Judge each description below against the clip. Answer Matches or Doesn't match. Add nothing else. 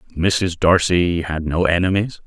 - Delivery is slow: Matches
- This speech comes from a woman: Doesn't match